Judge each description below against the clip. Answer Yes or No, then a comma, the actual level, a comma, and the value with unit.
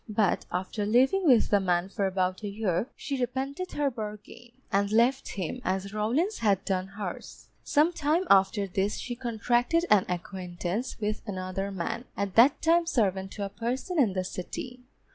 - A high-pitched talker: Yes, high, 210 Hz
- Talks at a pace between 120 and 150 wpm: No, average, 170 wpm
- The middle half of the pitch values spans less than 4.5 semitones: No, average, 4.8 semitones